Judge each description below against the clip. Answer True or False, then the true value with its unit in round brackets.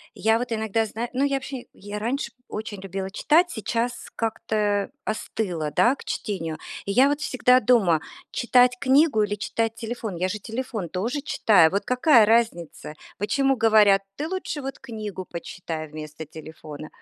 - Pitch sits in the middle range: False (220 Hz)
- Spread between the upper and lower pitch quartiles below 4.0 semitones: False (4.6 semitones)